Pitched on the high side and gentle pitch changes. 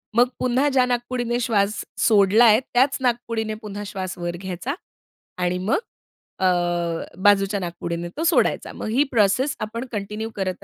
No: high, 215 Hz; average, 3.9 semitones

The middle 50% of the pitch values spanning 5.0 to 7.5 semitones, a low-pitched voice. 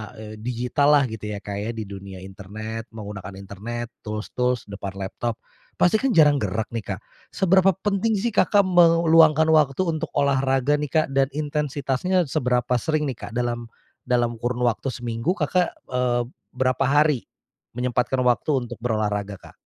Yes: wide, 5.6 semitones; low, 125 Hz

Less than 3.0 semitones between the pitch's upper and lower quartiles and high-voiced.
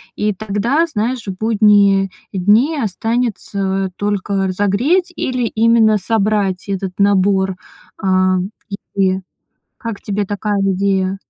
Yes: narrow, 2.5 semitones; high, 200 Hz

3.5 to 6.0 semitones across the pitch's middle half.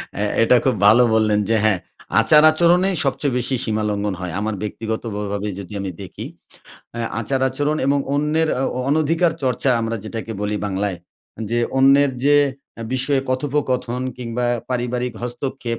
Yes: average, 4.3 semitones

